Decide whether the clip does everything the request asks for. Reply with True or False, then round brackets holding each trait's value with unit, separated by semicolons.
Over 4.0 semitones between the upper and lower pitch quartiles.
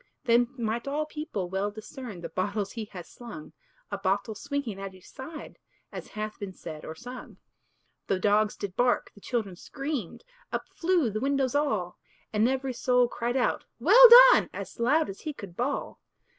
True (5.2 semitones)